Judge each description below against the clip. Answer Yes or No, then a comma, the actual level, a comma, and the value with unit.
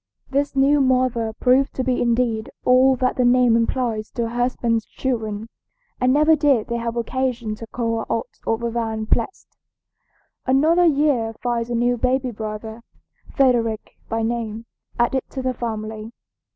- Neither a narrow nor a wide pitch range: No, narrow, 2.3 semitones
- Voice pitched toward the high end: Yes, high, 240 Hz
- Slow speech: No, average, 155 wpm